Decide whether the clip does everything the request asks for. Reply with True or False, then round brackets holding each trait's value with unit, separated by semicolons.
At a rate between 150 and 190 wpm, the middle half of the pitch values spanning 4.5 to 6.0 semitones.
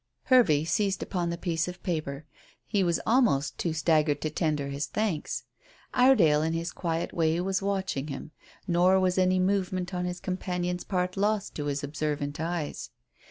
False (160 wpm; 3.4 semitones)